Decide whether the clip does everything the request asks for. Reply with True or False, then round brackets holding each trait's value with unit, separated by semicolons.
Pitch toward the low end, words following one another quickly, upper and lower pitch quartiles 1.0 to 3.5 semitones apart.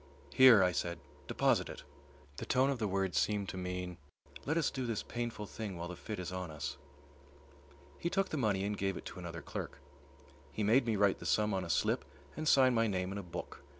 False (100 Hz; 220 wpm; 4.4 semitones)